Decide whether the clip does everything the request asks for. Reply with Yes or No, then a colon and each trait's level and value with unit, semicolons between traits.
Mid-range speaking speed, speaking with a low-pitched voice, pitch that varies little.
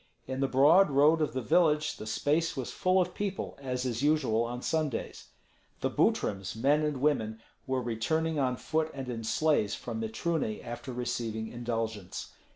No: average, 165 wpm; low, 130 Hz; average, 5.1 semitones